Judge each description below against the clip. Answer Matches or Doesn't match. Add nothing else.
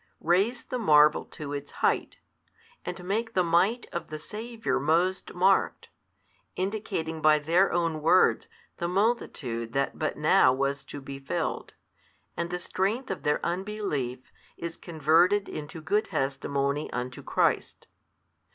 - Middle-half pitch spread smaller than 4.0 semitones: Doesn't match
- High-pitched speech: Doesn't match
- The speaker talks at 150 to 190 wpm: Doesn't match